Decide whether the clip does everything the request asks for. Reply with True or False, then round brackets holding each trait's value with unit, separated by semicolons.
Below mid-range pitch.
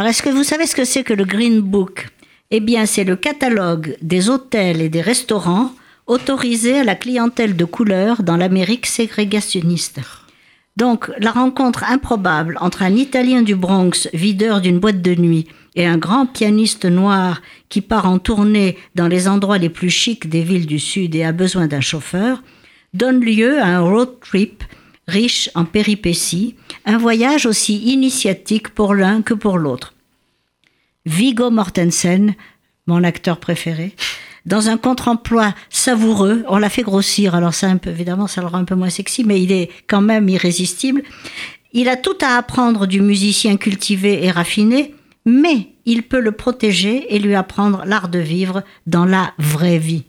False (205 Hz)